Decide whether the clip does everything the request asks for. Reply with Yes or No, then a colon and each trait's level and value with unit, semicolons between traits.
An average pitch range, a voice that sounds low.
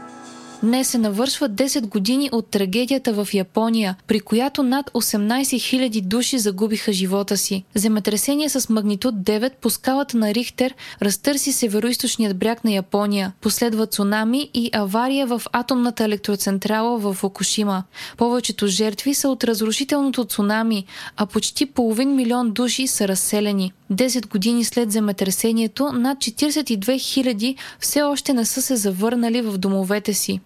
No: average, 3.6 semitones; high, 225 Hz